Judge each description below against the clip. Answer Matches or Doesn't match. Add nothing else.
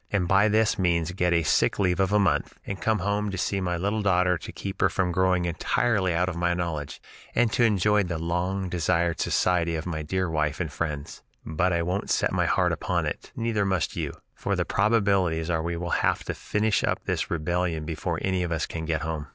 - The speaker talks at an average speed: Doesn't match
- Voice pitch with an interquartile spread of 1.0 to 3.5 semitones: Matches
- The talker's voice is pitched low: Matches